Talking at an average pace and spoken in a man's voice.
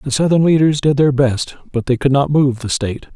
No: fast, 245 wpm; male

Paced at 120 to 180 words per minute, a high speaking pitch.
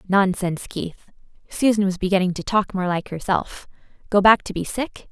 Yes: average, 175 wpm; high, 195 Hz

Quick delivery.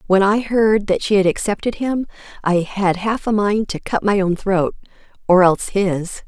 No: average, 190 wpm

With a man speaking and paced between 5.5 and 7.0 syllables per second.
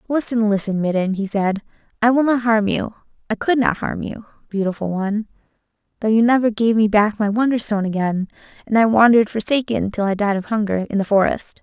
No: female; 5.9 syllables/s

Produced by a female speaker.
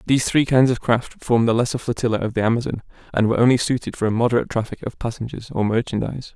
No: male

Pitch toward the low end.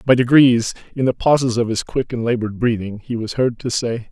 Yes: low, 120 Hz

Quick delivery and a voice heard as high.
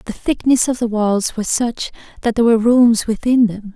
Yes: fast, 210 wpm; high, 230 Hz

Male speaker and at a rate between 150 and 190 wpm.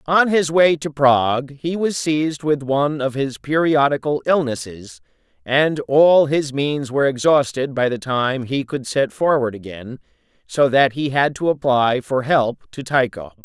Yes: male; average, 170 wpm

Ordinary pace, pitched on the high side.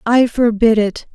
Yes: average, 155 wpm; high, 225 Hz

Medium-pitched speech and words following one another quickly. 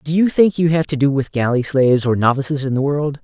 Yes: medium, 145 Hz; fast, 280 wpm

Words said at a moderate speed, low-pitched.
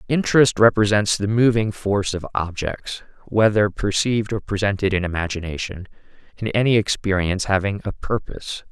No: slow, 115 wpm; low, 100 Hz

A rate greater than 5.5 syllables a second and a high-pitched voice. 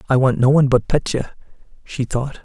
No: 5.7 syllables/s; low, 130 Hz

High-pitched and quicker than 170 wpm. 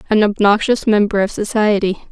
No: high, 210 Hz; average, 140 wpm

